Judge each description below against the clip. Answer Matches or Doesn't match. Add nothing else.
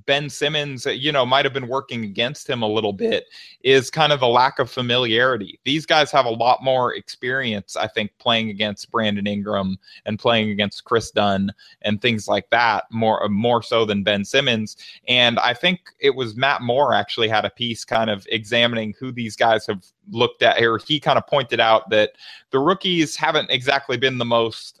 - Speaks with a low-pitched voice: Matches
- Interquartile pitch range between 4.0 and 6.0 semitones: Matches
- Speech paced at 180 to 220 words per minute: Matches